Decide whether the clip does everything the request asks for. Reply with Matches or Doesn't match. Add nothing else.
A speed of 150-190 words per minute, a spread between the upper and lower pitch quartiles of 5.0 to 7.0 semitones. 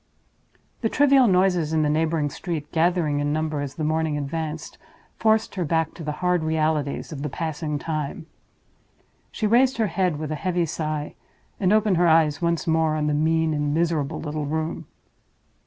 Doesn't match